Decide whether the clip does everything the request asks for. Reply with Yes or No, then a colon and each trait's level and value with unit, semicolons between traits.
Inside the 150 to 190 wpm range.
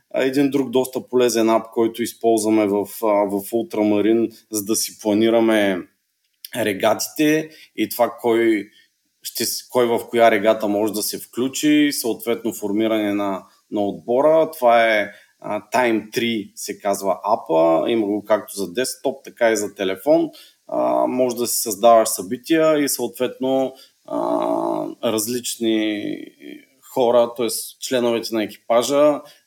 No: average, 125 wpm